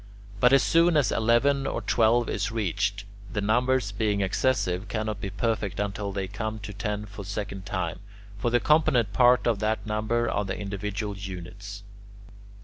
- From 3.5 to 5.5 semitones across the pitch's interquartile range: No, average, 2.9 semitones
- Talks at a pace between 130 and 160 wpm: No, average, 170 wpm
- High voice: No, low, 105 Hz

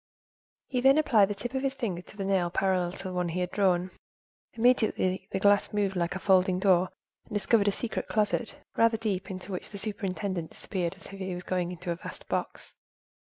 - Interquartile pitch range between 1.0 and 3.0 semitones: Yes, average, 2.7 semitones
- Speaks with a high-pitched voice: Yes, high, 195 Hz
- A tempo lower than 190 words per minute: No, average, 200 wpm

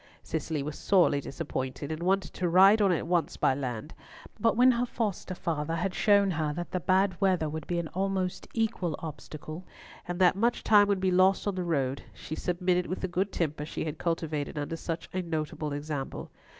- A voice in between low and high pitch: Yes, medium, 175 Hz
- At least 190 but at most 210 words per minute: Yes, average, 200 wpm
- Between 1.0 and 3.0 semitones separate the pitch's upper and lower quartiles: No, average, 3.7 semitones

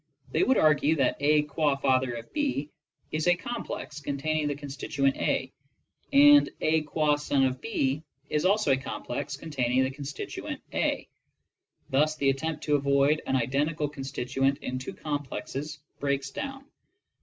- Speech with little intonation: Yes, narrow, 2.3 semitones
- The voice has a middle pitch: Yes, medium, 145 Hz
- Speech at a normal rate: Yes, average, 150 wpm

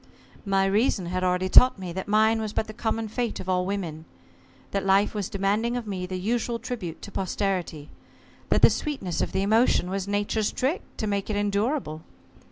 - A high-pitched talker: Yes, high, 200 Hz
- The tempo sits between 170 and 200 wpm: Yes, average, 190 wpm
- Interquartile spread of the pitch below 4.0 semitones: Yes, average, 3.0 semitones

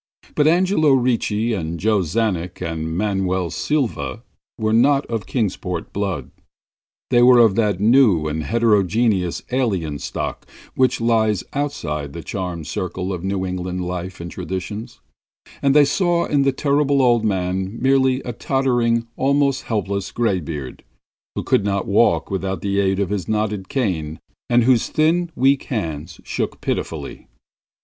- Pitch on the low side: Yes, low, 105 Hz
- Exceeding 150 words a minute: No, average, 145 wpm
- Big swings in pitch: Yes, wide, 5.7 semitones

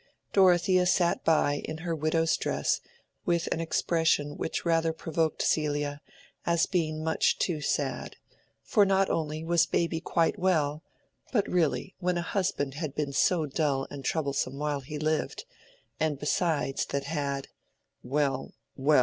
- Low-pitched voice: No, medium, 155 Hz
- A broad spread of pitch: No, average, 2.8 semitones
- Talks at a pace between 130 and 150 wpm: Yes, average, 140 wpm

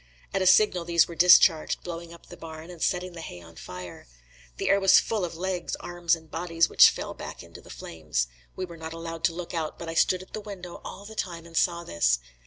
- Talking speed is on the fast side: Yes, fast, 240 wpm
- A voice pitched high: No, medium, 170 Hz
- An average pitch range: No, narrow, 1.8 semitones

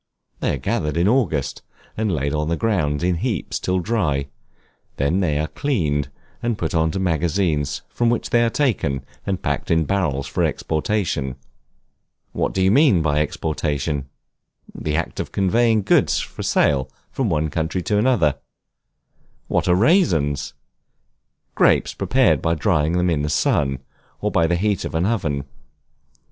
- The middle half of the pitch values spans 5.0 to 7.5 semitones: Yes, wide, 5.6 semitones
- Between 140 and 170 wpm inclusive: Yes, average, 155 wpm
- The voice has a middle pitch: No, very low, 85 Hz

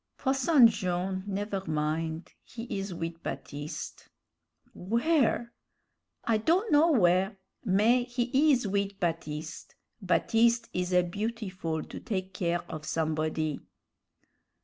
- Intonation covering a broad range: Yes, wide, 5.9 semitones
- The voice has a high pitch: Yes, high, 195 Hz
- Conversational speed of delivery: No, slow, 110 wpm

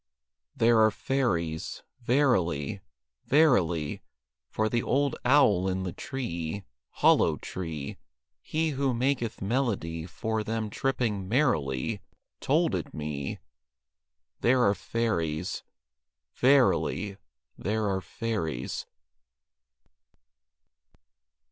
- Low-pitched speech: Yes, low, 110 Hz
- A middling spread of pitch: No, wide, 6.9 semitones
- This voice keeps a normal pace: No, slow, 90 wpm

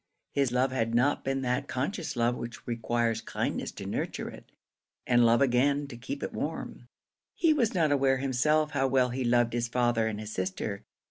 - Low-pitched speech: Yes, low, 125 Hz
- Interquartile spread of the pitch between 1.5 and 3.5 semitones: Yes, average, 2.8 semitones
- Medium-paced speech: Yes, average, 190 wpm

